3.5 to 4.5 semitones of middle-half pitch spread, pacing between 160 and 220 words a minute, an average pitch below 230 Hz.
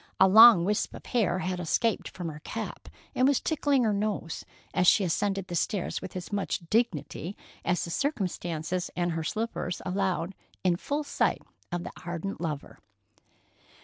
Yes: average, 3.8 semitones; average, 165 wpm; medium, 185 Hz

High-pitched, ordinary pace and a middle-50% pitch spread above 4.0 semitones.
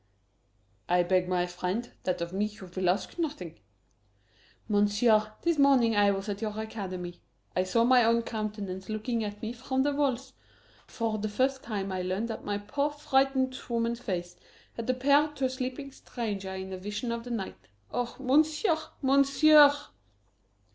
Yes: high, 225 Hz; average, 165 wpm; average, 5.1 semitones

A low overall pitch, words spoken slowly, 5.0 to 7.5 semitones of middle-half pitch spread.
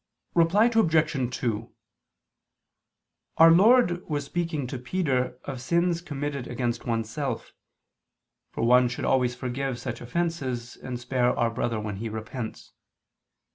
Yes: low, 130 Hz; slow, 125 wpm; average, 5.3 semitones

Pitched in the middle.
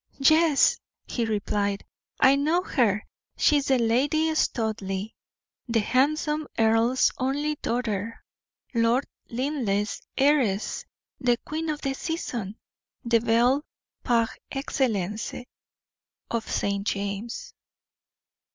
No: high, 240 Hz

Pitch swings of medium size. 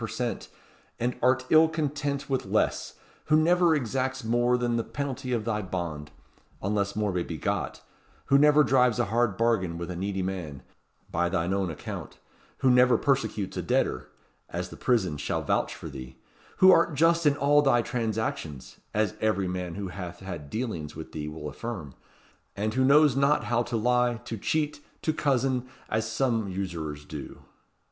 No: wide, 6.4 semitones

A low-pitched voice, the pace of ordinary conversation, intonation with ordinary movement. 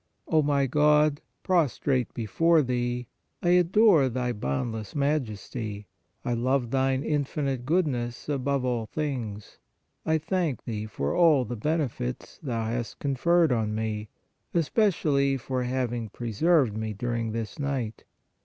No: low, 130 Hz; slow, 130 wpm; average, 4.6 semitones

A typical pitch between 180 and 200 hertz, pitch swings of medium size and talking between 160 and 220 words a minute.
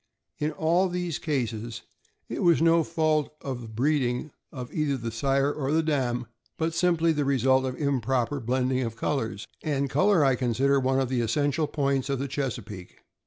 No: low, 135 Hz; average, 3.5 semitones; average, 165 wpm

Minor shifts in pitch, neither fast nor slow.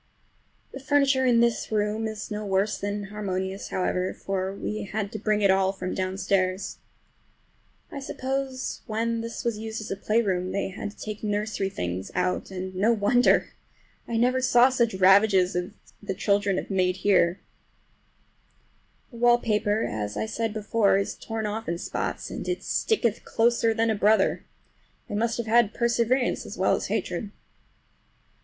No: average, 3.1 semitones; average, 160 wpm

